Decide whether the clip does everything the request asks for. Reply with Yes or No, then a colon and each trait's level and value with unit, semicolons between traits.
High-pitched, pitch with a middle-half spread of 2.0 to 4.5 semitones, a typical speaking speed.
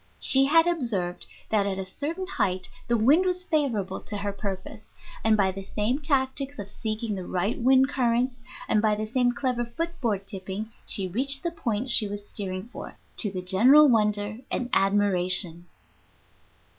No: high, 220 Hz; average, 5.1 semitones; average, 170 wpm